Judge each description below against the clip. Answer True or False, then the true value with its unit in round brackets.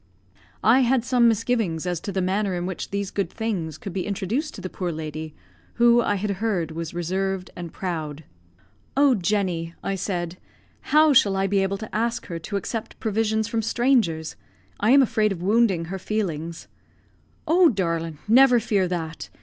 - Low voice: False (195 Hz)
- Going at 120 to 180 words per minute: True (175 wpm)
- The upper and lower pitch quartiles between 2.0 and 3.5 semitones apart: False (4.5 semitones)